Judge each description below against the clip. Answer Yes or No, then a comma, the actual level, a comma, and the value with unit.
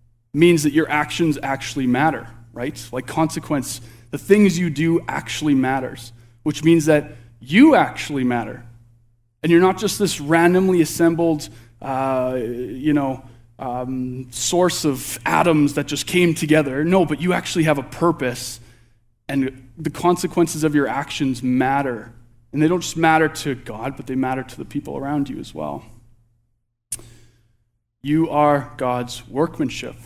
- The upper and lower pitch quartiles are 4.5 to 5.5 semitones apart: Yes, average, 5.1 semitones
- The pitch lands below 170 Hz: Yes, low, 135 Hz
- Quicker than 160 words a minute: No, average, 150 wpm